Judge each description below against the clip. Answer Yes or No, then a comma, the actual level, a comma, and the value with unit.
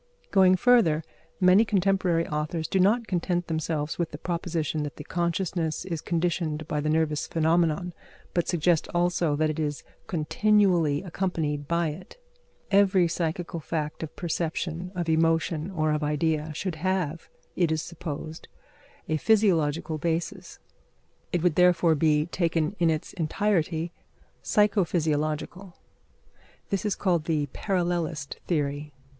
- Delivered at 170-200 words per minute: No, slow, 135 wpm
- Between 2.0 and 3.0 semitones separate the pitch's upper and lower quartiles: Yes, narrow, 2.6 semitones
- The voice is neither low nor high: Yes, medium, 165 Hz